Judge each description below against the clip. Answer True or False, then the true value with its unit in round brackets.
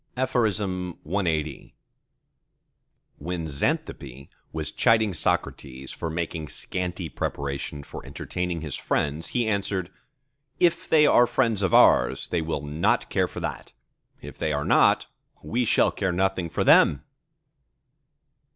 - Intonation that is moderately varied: False (5.7 semitones)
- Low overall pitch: True (90 Hz)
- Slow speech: True (120 wpm)